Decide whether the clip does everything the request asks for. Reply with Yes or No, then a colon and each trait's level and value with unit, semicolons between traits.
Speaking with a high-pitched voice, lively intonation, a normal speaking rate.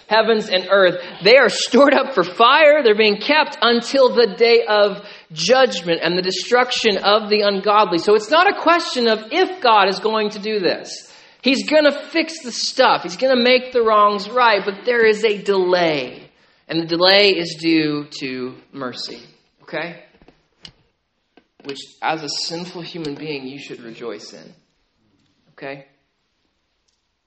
Yes: high, 210 Hz; wide, 6.0 semitones; average, 160 wpm